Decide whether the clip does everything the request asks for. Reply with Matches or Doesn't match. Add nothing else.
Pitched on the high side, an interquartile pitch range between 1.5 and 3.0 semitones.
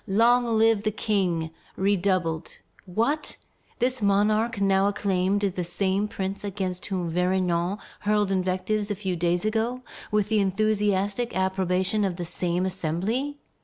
Matches